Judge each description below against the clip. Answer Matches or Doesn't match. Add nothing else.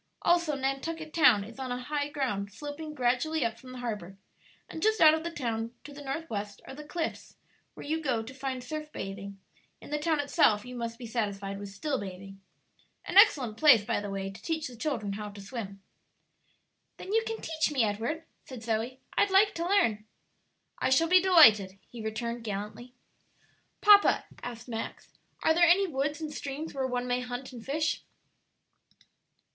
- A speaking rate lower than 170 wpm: Doesn't match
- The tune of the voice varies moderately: Doesn't match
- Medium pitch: Doesn't match